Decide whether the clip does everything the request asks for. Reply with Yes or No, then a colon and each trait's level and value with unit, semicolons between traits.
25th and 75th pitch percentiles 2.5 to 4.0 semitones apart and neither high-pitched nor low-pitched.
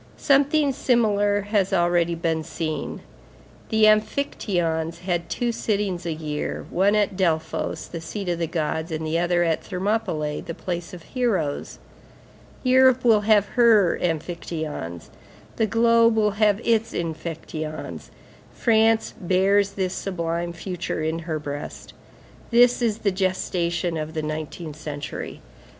No: average, 4.8 semitones; medium, 180 Hz